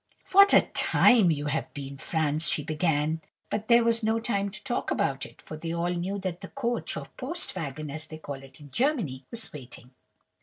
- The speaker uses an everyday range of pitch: No, wide, 7.3 semitones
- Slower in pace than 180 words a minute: No, fast, 205 wpm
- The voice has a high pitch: No, medium, 165 Hz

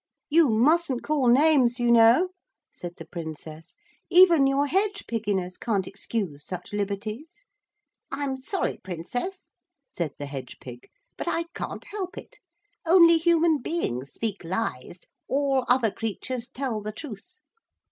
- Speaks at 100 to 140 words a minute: Yes, slow, 135 wpm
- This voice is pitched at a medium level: No, high, 240 Hz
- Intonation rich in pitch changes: Yes, wide, 8.7 semitones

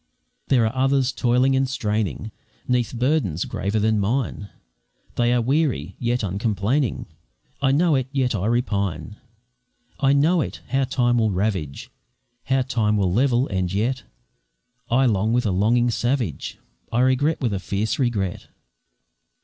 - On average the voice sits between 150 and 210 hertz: No, low, 120 Hz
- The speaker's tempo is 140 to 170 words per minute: Yes, average, 145 wpm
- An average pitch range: Yes, average, 4.3 semitones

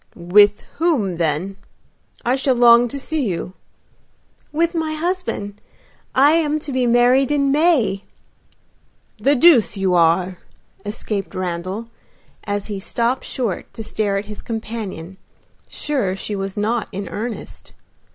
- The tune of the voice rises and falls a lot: Yes, wide, 5.8 semitones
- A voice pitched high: Yes, high, 225 Hz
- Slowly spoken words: Yes, slow, 130 wpm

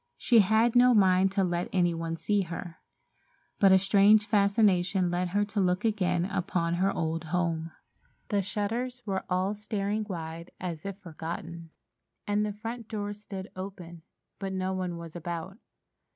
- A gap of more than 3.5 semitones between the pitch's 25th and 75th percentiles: No, average, 2.9 semitones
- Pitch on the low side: No, high, 190 Hz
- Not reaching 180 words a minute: Yes, average, 160 wpm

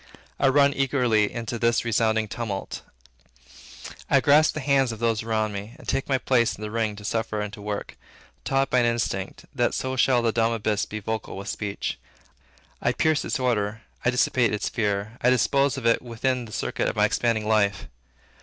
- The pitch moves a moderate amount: Yes, average, 3.0 semitones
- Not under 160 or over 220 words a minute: Yes, average, 195 wpm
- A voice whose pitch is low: Yes, low, 115 Hz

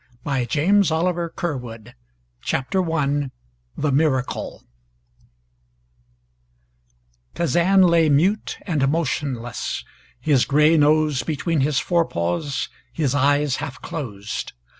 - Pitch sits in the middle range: Yes, medium, 150 Hz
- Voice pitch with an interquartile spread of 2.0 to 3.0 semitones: No, average, 3.7 semitones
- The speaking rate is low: Yes, slow, 95 wpm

